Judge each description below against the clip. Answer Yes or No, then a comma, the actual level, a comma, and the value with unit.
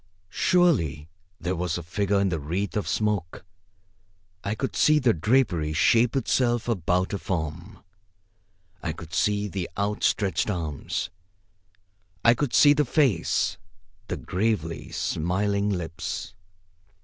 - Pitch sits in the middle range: No, low, 100 Hz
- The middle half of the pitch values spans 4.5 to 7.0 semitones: Yes, average, 4.9 semitones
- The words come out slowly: Yes, slow, 125 wpm